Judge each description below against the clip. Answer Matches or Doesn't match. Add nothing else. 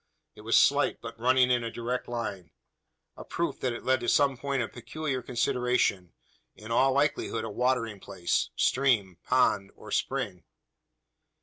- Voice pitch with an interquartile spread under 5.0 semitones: Matches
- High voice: Doesn't match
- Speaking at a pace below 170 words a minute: Matches